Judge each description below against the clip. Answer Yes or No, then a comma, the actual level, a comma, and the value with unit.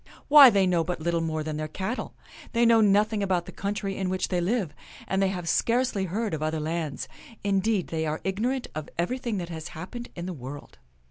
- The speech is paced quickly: Yes, fast, 215 wpm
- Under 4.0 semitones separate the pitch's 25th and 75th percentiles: No, average, 4.7 semitones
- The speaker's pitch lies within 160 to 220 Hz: Yes, medium, 185 Hz